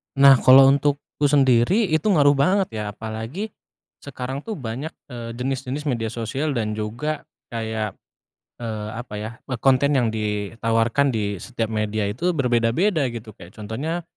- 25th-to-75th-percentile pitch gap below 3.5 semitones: No, average, 4.2 semitones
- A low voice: Yes, low, 125 Hz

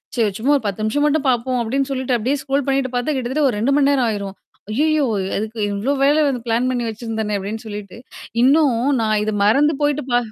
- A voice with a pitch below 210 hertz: No, very high, 250 Hz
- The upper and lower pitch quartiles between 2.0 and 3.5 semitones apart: No, average, 4.2 semitones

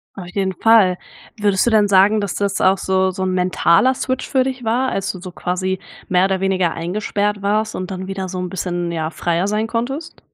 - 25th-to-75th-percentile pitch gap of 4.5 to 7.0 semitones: No, narrow, 2.6 semitones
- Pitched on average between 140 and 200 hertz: Yes, high, 190 Hz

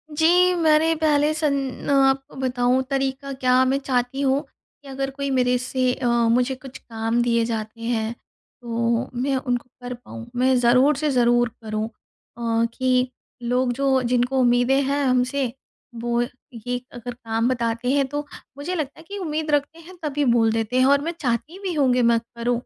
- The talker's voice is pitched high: Yes, very high, 255 Hz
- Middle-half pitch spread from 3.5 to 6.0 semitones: No, average, 2.7 semitones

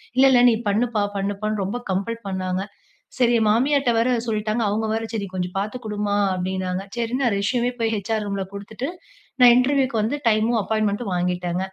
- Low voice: No, high, 215 Hz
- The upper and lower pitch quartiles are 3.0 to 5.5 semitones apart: Yes, average, 3.4 semitones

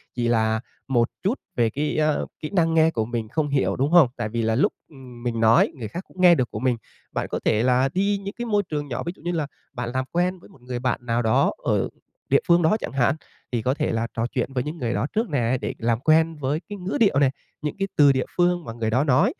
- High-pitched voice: No, low, 135 Hz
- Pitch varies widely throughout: Yes, wide, 5.8 semitones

